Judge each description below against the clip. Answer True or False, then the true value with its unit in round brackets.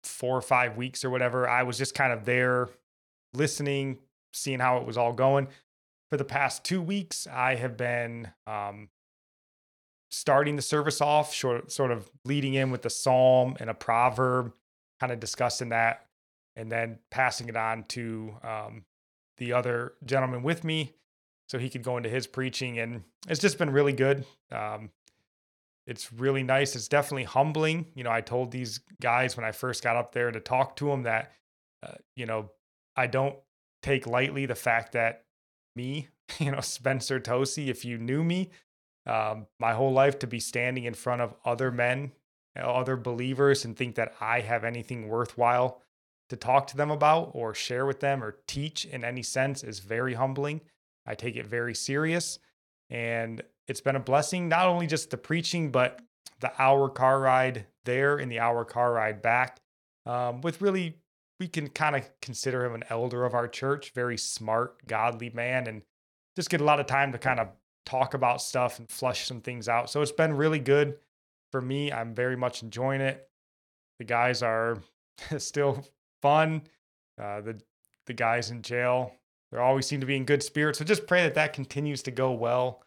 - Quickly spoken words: False (185 wpm)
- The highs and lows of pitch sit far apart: False (2.9 semitones)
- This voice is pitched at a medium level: False (125 Hz)